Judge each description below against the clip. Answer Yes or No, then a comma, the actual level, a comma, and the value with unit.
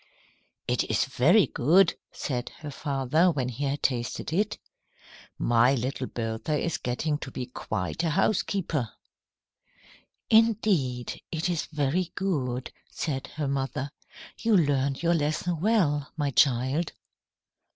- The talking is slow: Yes, slow, 125 wpm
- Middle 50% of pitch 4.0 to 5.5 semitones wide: Yes, average, 4.8 semitones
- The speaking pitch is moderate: Yes, medium, 145 Hz